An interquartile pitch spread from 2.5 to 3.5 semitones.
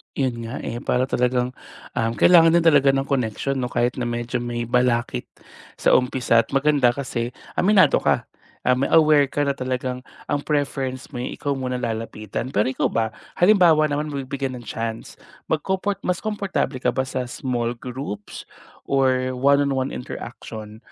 Yes: average, 2.9 semitones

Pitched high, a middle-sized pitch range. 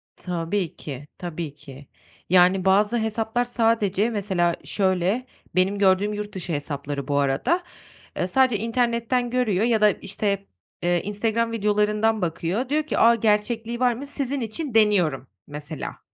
Yes: high, 210 Hz; average, 4.6 semitones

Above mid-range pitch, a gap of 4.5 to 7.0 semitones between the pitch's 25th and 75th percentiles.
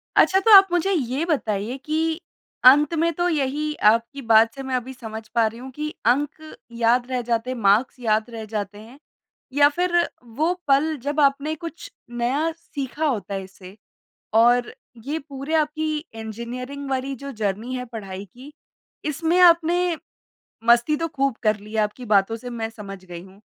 Yes: very high, 255 Hz; average, 5.3 semitones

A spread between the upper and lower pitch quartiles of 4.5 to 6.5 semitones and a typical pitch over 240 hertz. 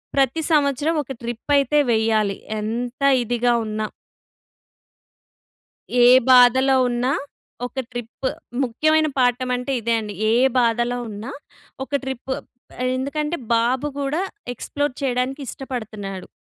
No: average, 2.8 semitones; very high, 250 Hz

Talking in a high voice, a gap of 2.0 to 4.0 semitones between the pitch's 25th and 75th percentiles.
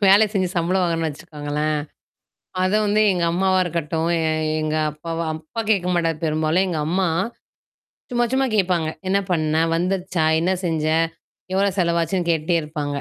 No: medium, 170 Hz; average, 2.9 semitones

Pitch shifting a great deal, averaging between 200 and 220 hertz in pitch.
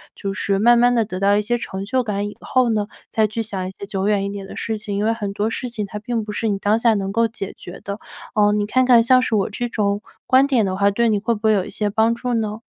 No: narrow, 2.4 semitones; high, 210 Hz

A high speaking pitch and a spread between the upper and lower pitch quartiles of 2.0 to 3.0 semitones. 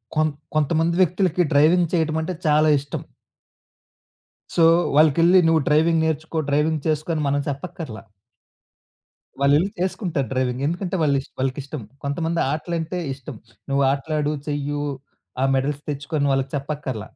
No: medium, 150 Hz; average, 2.7 semitones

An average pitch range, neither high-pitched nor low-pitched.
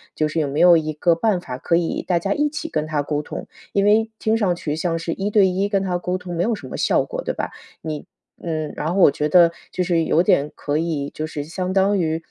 Yes: average, 3.8 semitones; medium, 170 Hz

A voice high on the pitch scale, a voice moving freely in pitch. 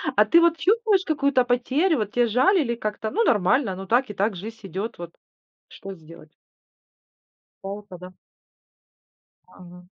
Yes: high, 225 Hz; wide, 7.0 semitones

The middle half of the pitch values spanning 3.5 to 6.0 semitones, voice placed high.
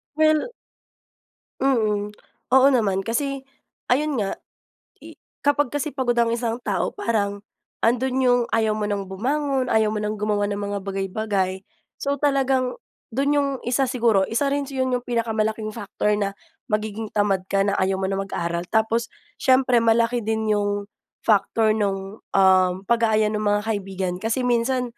Yes: average, 3.8 semitones; high, 220 Hz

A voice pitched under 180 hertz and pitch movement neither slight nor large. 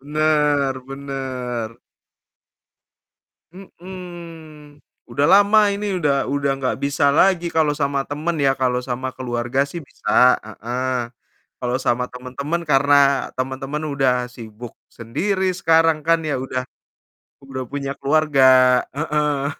Yes: medium, 140 Hz; average, 3.3 semitones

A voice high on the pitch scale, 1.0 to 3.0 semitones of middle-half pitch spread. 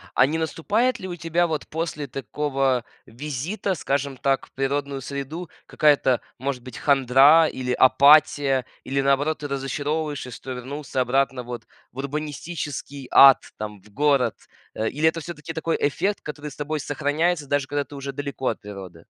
No: medium, 140 Hz; narrow, 2.5 semitones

